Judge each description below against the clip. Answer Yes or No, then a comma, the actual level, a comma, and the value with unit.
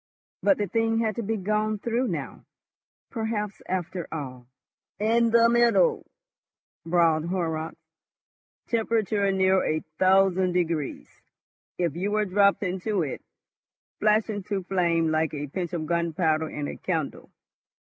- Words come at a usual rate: No, slow, 130 wpm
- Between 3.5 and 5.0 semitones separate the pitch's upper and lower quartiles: Yes, average, 4.4 semitones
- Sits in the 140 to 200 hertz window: Yes, high, 190 Hz